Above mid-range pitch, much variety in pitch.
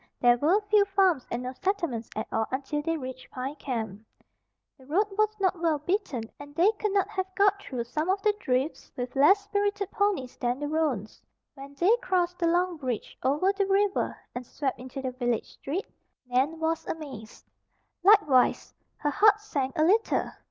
Yes: very high, 310 Hz; wide, 7.3 semitones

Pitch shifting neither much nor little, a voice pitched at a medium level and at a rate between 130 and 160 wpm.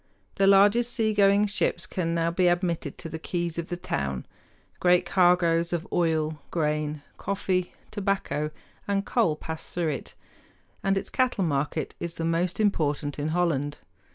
Yes: average, 3.8 semitones; medium, 170 Hz; average, 155 wpm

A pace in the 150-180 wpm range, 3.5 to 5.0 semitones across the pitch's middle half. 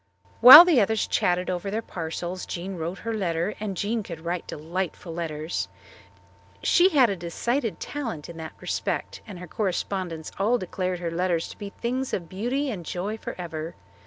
Yes: average, 170 wpm; average, 4.6 semitones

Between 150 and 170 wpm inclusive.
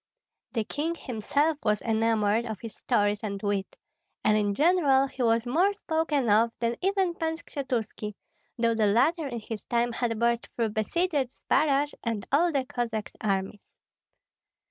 Yes: average, 155 wpm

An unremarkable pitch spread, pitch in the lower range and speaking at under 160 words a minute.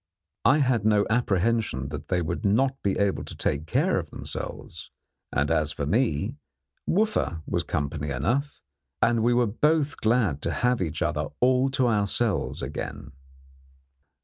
No: wide, 7.9 semitones; low, 105 Hz; average, 150 wpm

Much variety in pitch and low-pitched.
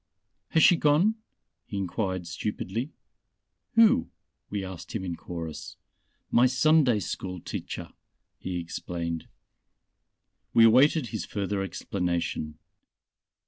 Yes: wide, 6.4 semitones; low, 100 Hz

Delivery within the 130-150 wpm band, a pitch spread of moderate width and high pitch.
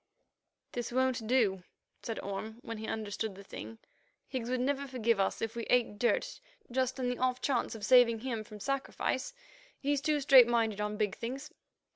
No: average, 180 wpm; average, 3.0 semitones; high, 240 Hz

